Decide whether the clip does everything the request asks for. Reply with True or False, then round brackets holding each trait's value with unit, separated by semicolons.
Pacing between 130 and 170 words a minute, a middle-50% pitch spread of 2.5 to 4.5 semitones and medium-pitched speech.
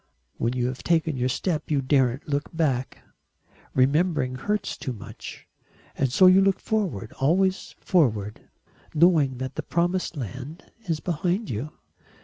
False (140 wpm; 5.5 semitones; 150 Hz)